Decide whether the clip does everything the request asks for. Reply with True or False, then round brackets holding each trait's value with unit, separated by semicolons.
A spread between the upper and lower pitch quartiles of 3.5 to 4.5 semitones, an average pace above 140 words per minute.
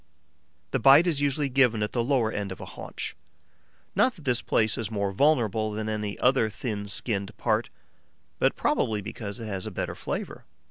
True (3.8 semitones; 185 wpm)